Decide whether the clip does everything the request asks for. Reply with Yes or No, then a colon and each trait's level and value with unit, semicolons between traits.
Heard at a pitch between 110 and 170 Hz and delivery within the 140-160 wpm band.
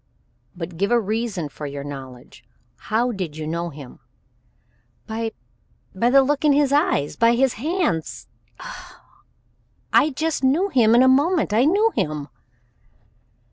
No: high, 230 Hz; average, 145 wpm